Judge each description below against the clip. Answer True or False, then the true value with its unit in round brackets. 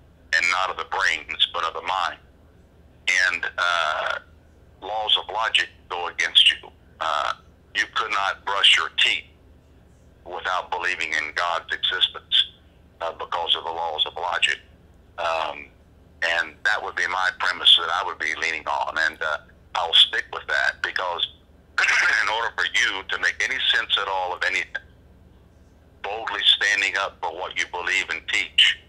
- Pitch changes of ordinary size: False (1.8 semitones)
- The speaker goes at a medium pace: True (160 wpm)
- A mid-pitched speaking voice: False (85 Hz)